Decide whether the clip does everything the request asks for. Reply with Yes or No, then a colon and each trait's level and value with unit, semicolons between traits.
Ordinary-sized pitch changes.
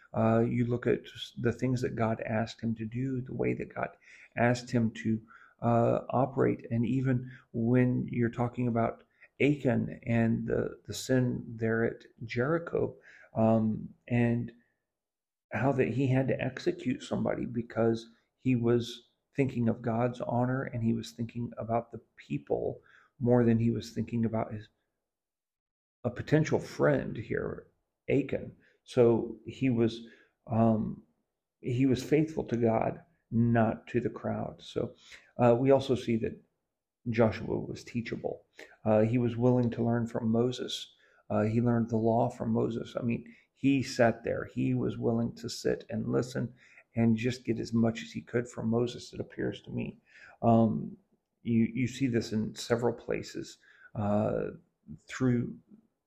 No: narrow, 1.5 semitones